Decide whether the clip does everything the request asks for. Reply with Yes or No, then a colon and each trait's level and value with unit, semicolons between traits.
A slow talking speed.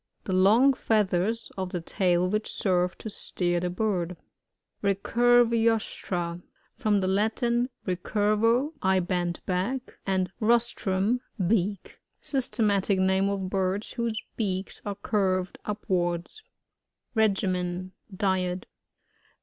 Yes: slow, 110 wpm